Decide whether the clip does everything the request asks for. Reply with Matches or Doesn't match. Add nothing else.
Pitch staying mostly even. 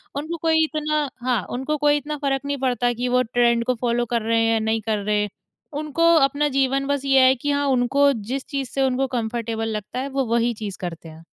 Doesn't match